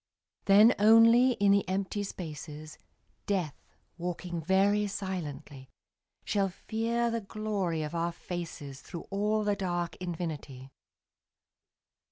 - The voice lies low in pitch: No, high, 190 Hz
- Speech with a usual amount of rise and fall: Yes, average, 4.0 semitones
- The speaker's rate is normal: No, slow, 110 wpm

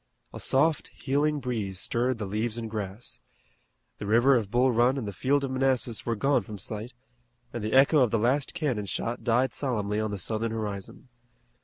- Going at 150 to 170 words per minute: No, average, 190 wpm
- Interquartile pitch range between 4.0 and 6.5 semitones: No, average, 3.6 semitones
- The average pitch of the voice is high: No, low, 120 Hz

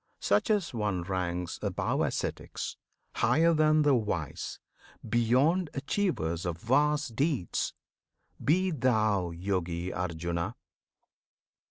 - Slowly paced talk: Yes, slow, 95 wpm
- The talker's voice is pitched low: Yes, low, 110 Hz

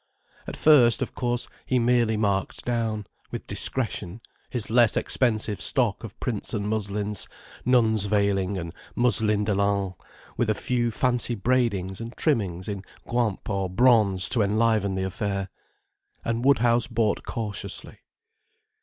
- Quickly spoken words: No, slow, 135 wpm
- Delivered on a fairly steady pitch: No, average, 3.1 semitones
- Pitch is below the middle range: Yes, low, 110 Hz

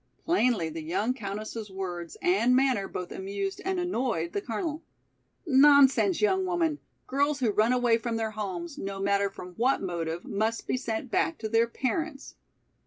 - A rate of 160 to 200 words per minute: Yes, average, 165 wpm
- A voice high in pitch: Yes, high, 230 Hz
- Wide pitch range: Yes, wide, 5.8 semitones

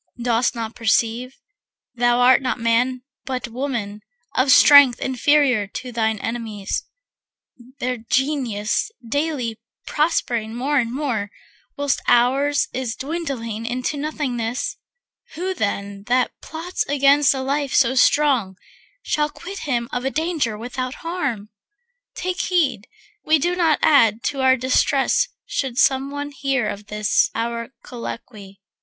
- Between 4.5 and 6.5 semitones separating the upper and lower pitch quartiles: No, average, 3.7 semitones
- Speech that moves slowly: Yes, slow, 130 wpm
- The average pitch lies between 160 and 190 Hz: No, very high, 255 Hz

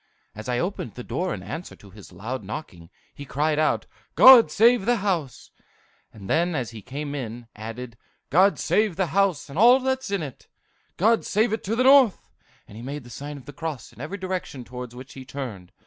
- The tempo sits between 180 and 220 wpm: Yes, fast, 205 wpm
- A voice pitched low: No, medium, 145 Hz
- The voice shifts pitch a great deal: Yes, wide, 8.2 semitones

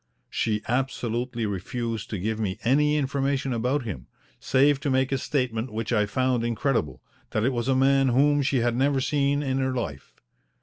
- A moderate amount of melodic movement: Yes, average, 3.1 semitones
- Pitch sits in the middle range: No, low, 130 Hz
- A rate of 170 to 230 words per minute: Yes, average, 180 wpm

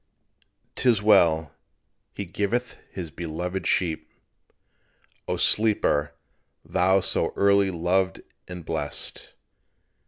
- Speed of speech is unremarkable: No, slow, 90 wpm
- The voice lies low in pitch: Yes, very low, 90 Hz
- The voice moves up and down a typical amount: Yes, average, 3.5 semitones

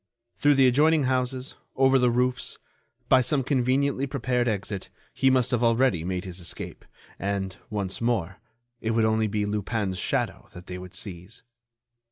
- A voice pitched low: Yes, low, 115 Hz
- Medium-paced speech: Yes, average, 160 wpm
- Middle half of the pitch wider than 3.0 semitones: Yes, average, 4.9 semitones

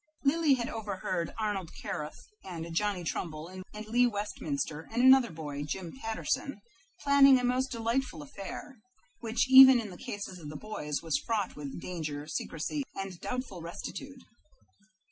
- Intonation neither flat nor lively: No, wide, 7.2 semitones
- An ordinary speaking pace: Yes, average, 145 wpm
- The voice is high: Yes, high, 205 Hz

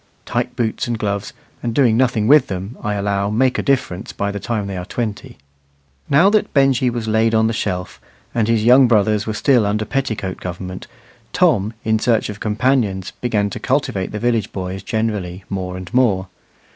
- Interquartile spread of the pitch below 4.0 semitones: Yes, average, 3.5 semitones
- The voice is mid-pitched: No, low, 110 Hz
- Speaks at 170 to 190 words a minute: Yes, average, 185 wpm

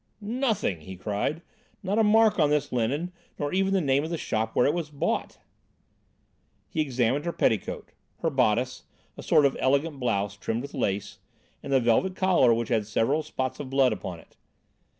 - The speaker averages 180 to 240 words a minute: Yes, average, 185 wpm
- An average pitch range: No, wide, 6.5 semitones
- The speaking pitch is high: No, medium, 140 Hz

